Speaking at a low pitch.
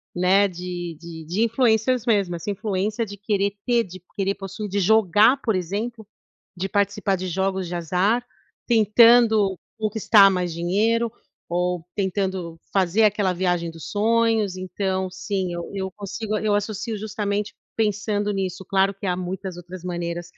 No: high, 195 Hz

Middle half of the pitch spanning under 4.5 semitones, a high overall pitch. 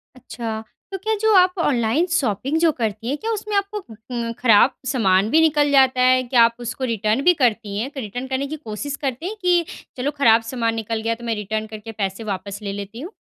No: average, 5.1 semitones; high, 245 Hz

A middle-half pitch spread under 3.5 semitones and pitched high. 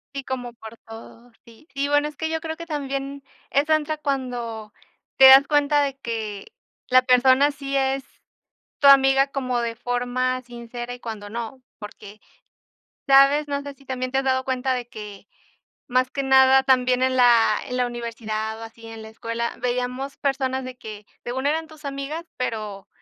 Yes: average, 2.8 semitones; very high, 255 Hz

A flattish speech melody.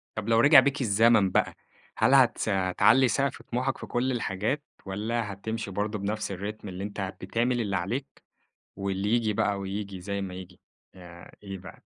No: average, 3.4 semitones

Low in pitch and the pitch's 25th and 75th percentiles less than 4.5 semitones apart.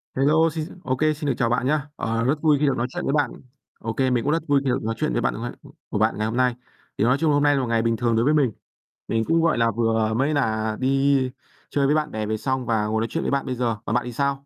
Yes: low, 130 Hz; average, 3.9 semitones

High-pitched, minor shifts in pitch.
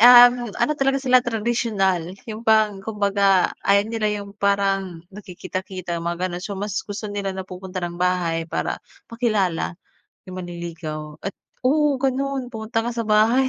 No: high, 200 Hz; average, 4.3 semitones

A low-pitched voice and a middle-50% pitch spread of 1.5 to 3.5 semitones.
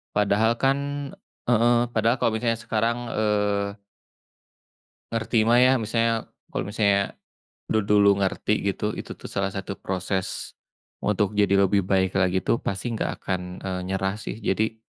Yes: low, 105 Hz; average, 2.7 semitones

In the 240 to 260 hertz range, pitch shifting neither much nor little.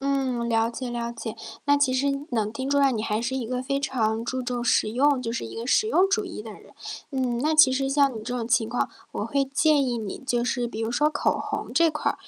Yes: very high, 255 Hz; average, 3.1 semitones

